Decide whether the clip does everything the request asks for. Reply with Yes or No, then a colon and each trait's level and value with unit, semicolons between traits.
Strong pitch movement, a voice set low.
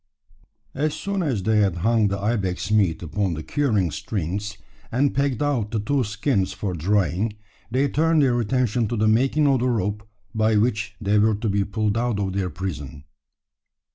No: average, 3.8 semitones; low, 105 Hz